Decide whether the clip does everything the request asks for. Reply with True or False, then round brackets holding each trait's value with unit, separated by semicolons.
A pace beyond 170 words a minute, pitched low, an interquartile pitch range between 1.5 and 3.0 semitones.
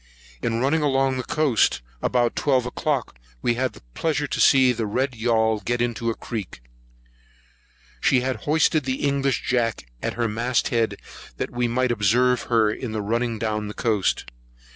False (165 wpm; 120 Hz; 2.7 semitones)